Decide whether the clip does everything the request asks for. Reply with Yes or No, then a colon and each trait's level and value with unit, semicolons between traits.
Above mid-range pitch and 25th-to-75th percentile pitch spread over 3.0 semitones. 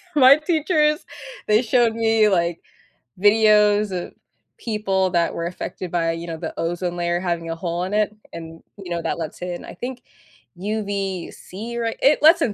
Yes: high, 195 Hz; average, 4.5 semitones